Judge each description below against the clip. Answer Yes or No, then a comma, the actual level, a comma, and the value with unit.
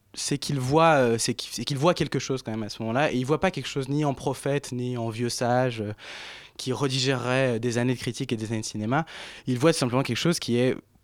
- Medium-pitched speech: No, low, 130 Hz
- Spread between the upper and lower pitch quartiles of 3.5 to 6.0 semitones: No, average, 3.0 semitones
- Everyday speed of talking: No, fast, 245 wpm